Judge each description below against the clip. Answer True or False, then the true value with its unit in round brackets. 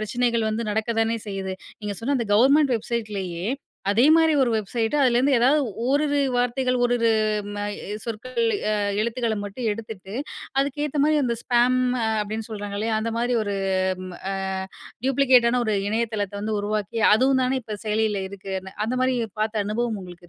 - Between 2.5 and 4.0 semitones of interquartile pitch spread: True (3.0 semitones)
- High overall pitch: True (230 Hz)